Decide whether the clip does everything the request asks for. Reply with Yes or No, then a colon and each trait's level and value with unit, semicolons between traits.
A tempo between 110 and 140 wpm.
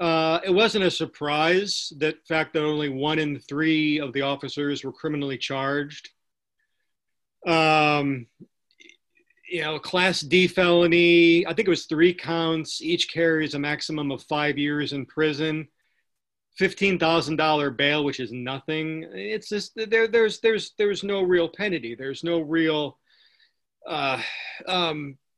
Yes: slow, 135 wpm